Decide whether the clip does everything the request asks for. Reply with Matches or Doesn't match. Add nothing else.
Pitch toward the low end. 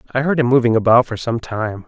Matches